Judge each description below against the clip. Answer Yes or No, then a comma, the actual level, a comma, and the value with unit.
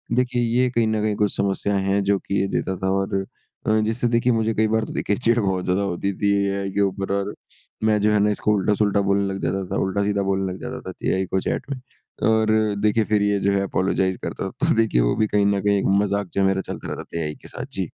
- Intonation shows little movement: Yes, narrow, 1.9 semitones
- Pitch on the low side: Yes, low, 100 Hz